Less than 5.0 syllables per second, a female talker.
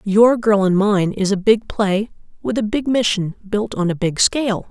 Yes: 4.5 syllables/s; female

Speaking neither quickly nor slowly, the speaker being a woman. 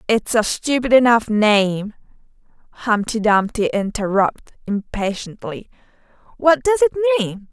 No: slow, 105 wpm; female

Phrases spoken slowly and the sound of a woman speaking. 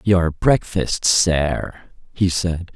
No: slow, 110 wpm; male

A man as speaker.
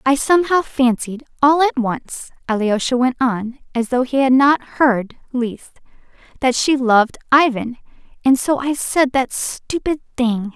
No: female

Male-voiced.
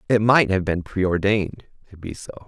Yes: male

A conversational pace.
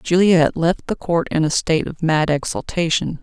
Yes: average, 185 wpm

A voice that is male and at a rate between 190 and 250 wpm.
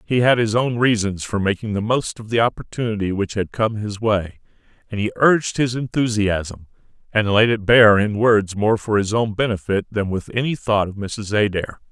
Yes: male; average, 200 wpm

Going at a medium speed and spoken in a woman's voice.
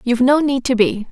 No: fast, 270 wpm; female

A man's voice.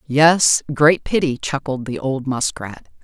No: female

